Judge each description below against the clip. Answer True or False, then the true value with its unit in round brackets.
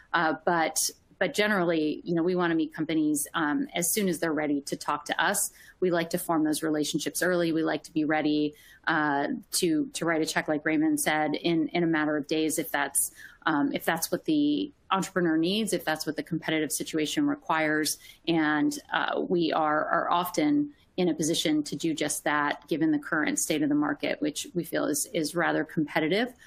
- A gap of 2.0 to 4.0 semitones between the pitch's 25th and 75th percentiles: True (2.6 semitones)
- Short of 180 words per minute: False (205 wpm)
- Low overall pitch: False (160 Hz)